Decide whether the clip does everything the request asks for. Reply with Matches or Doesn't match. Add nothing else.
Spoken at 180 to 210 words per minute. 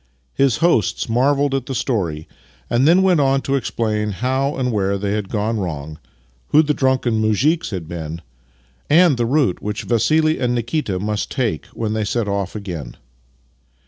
Doesn't match